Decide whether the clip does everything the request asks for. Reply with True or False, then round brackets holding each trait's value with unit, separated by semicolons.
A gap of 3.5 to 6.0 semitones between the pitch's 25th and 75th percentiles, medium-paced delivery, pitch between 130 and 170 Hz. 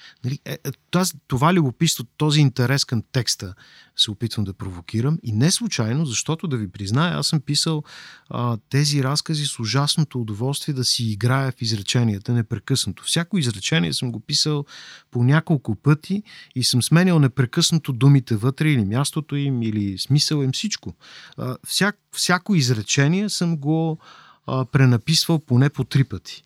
True (4.6 semitones; 145 wpm; 140 Hz)